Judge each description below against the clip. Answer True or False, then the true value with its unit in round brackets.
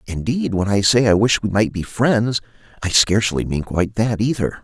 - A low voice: True (105 Hz)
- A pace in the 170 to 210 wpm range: True (205 wpm)